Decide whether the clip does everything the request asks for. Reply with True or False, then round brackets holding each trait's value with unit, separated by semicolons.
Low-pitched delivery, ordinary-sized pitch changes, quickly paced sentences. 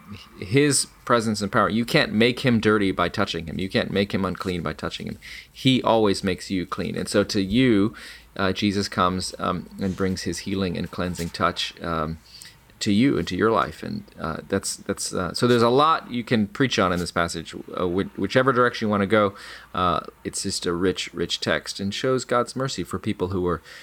True (100 Hz; 3.9 semitones; 215 wpm)